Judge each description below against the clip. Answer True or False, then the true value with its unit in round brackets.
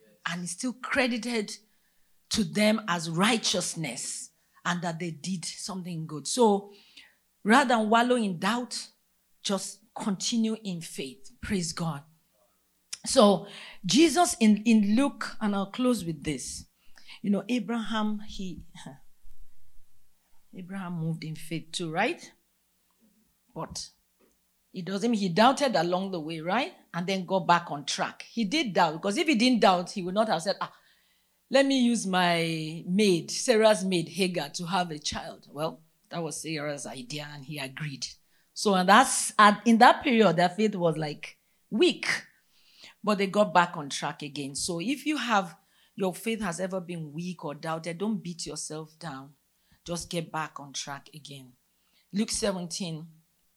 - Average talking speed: True (155 wpm)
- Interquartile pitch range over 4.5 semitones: True (5.2 semitones)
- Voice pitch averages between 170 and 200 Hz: True (185 Hz)